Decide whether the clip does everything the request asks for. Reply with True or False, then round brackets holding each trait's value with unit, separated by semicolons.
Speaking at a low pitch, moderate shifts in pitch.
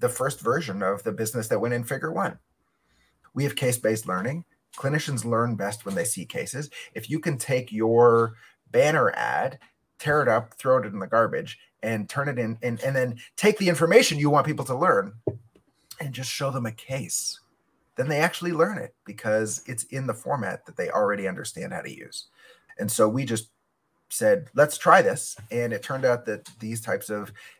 True (125 Hz; 4.6 semitones)